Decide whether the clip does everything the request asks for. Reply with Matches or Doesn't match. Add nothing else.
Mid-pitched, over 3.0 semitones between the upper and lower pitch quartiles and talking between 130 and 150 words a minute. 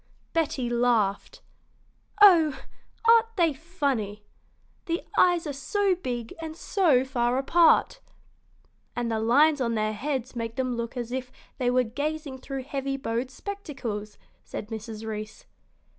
Doesn't match